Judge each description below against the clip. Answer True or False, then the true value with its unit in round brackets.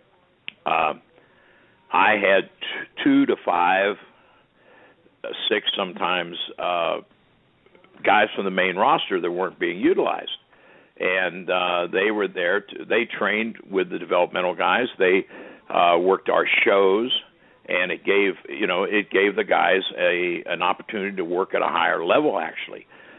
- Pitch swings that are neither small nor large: True (3.4 semitones)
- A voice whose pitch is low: False (395 Hz)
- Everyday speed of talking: True (145 wpm)